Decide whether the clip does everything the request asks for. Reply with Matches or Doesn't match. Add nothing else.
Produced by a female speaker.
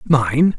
Doesn't match